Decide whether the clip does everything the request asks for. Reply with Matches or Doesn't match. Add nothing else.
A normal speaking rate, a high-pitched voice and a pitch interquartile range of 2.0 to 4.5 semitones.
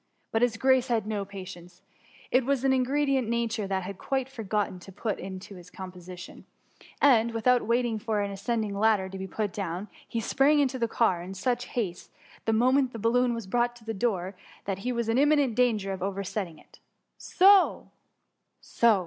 Matches